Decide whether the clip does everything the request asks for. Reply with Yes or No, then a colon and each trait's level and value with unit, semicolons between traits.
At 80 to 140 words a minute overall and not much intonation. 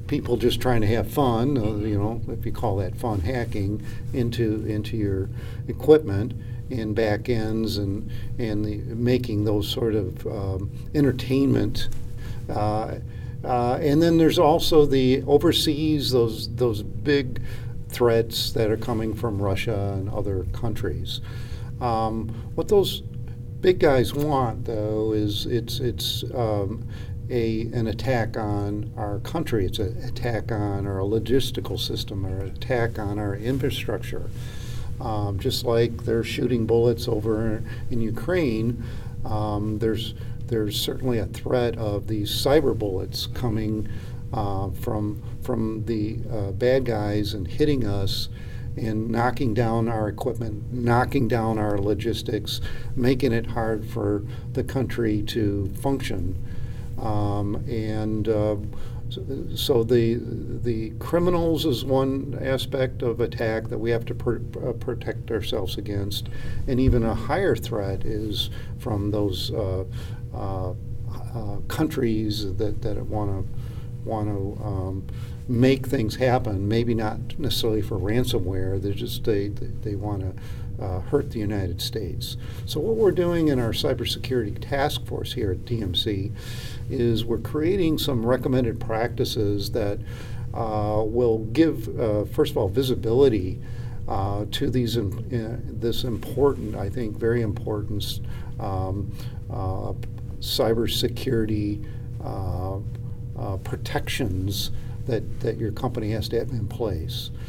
Yes: slow, 135 wpm; narrow, 2.2 semitones